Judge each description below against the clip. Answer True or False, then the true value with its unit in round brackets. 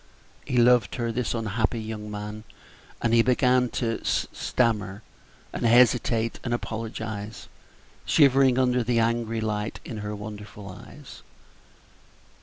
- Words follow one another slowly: True (120 wpm)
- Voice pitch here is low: True (115 Hz)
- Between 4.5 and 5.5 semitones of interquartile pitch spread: False (2.4 semitones)